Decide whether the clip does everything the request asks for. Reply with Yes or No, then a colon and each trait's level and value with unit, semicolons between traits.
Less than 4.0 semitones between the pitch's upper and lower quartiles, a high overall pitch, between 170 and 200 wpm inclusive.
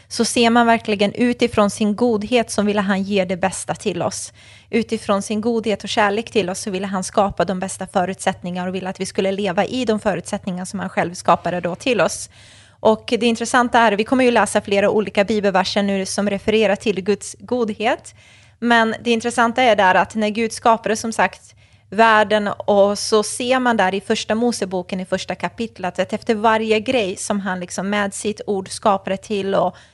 Yes: average, 2.8 semitones; high, 210 Hz; fast, 195 wpm